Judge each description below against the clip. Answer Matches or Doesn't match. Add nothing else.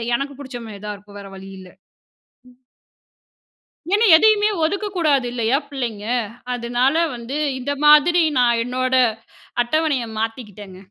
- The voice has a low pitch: Doesn't match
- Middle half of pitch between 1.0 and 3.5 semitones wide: Doesn't match